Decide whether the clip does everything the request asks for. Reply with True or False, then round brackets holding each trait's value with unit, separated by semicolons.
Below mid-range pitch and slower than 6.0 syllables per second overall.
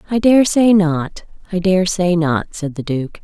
False (180 Hz; 4.1 syllables/s)